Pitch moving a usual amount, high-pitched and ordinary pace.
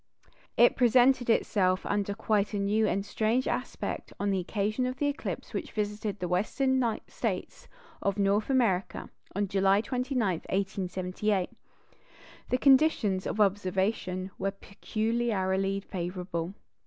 No: average, 3.4 semitones; high, 205 Hz; slow, 120 wpm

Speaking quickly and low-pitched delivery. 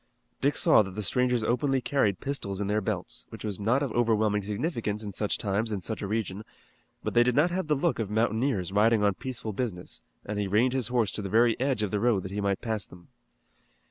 Yes: fast, 235 wpm; low, 110 Hz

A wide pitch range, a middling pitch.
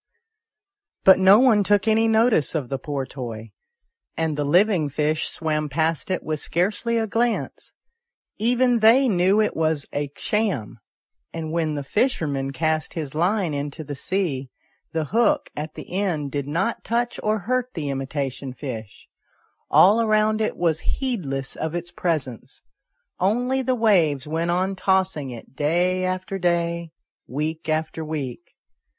Yes: wide, 6.2 semitones; medium, 170 Hz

